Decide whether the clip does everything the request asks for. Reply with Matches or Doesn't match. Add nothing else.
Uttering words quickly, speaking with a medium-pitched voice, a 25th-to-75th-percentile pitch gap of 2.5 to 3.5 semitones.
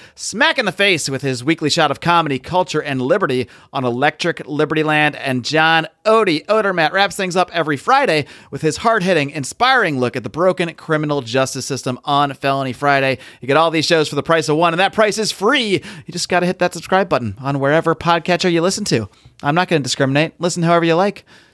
Doesn't match